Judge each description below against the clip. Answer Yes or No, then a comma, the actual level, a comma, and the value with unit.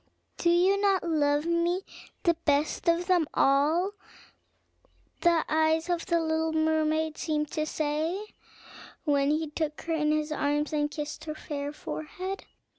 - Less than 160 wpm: Yes, average, 145 wpm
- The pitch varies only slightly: Yes, narrow, 2.1 semitones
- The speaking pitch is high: Yes, very high, 315 Hz